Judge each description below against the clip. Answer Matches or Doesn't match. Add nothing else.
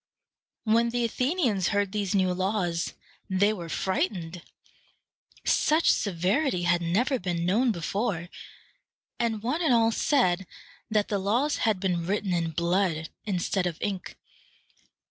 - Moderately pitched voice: Doesn't match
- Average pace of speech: Doesn't match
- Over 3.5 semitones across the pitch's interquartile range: Matches